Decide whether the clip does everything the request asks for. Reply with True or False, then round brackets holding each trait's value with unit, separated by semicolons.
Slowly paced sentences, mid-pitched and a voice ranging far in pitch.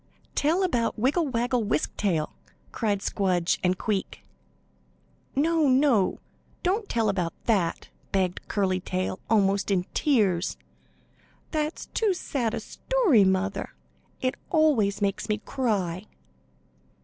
False (115 wpm; 215 Hz; 6.8 semitones)